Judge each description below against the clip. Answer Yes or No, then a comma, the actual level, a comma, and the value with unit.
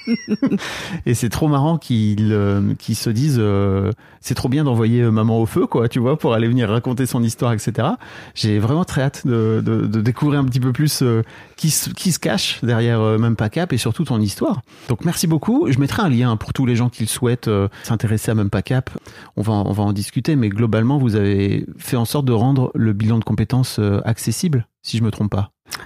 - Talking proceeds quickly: Yes, fast, 230 wpm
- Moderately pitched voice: No, low, 120 Hz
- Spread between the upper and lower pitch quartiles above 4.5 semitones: No, average, 3.7 semitones